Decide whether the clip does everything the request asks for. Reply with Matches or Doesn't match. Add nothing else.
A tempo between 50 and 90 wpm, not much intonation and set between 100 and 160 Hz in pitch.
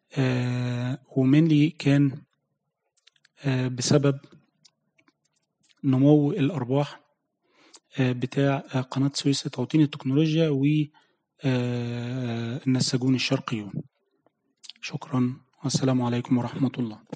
Matches